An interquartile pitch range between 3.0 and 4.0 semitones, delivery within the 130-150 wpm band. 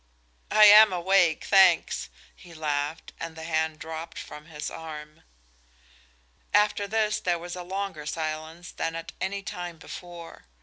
Yes: average, 3.3 semitones; average, 140 wpm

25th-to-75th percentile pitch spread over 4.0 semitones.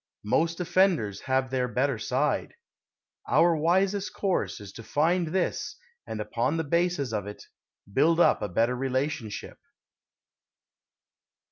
Yes: wide, 5.6 semitones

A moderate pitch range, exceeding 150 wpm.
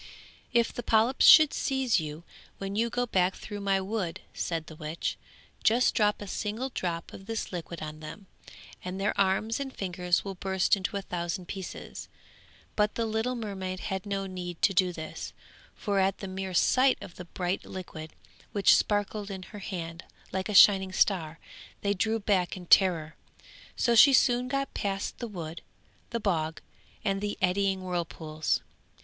Yes: average, 3.0 semitones; average, 170 wpm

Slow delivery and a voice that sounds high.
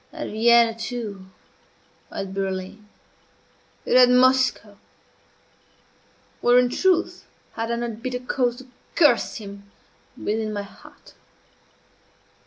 Yes: slow, 105 wpm; high, 230 Hz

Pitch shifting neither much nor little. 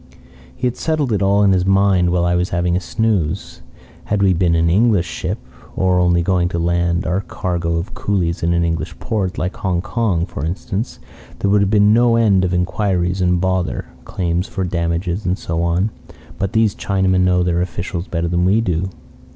No: narrow, 2.3 semitones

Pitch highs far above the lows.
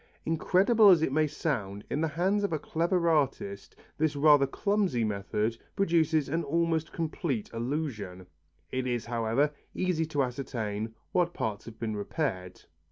Yes: wide, 6.4 semitones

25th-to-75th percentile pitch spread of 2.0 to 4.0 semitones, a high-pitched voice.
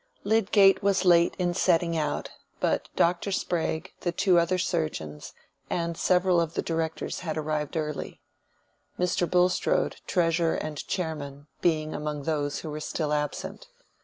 No: average, 2.7 semitones; medium, 165 Hz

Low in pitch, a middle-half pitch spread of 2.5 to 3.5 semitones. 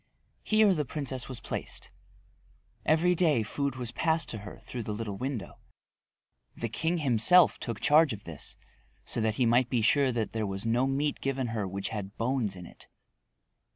No: low, 120 Hz; average, 4.7 semitones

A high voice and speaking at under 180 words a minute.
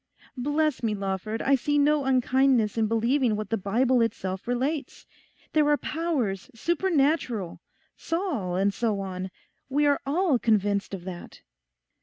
Yes: high, 245 Hz; average, 140 wpm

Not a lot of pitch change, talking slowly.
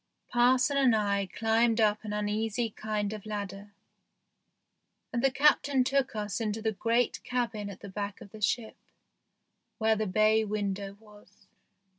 No: narrow, 2.2 semitones; average, 150 wpm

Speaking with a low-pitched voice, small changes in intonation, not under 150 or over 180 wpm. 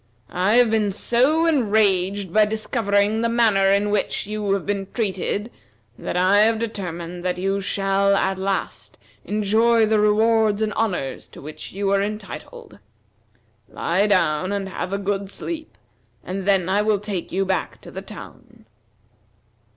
No: high, 200 Hz; narrow, 2.1 semitones; average, 155 wpm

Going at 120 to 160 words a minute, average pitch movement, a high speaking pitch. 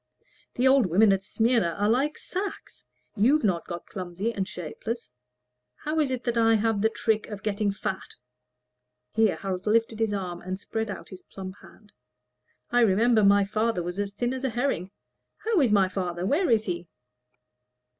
No: average, 175 wpm; average, 3.6 semitones; high, 210 Hz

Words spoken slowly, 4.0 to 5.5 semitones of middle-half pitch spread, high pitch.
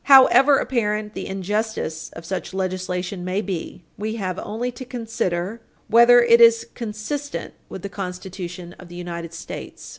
No: average, 150 wpm; average, 4.3 semitones; high, 205 Hz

